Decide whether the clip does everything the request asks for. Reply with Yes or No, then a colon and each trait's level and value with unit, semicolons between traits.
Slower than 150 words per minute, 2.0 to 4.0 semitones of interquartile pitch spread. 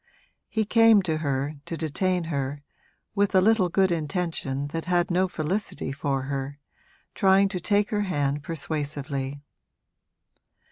No: slow, 135 wpm; average, 5.0 semitones